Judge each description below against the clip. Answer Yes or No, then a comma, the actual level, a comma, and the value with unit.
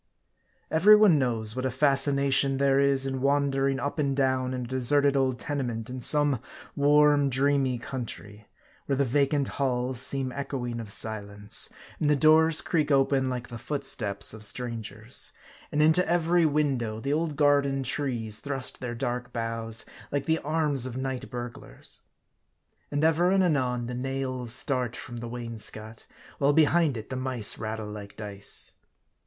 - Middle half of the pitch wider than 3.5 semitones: No, average, 3.2 semitones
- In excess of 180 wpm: No, average, 160 wpm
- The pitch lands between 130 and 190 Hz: Yes, low, 135 Hz